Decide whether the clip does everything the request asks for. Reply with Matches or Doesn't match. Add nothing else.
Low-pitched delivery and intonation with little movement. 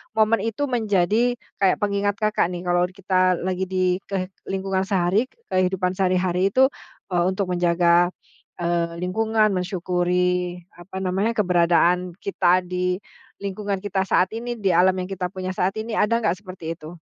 Doesn't match